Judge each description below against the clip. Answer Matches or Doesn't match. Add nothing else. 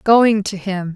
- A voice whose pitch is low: Doesn't match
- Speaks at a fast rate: Doesn't match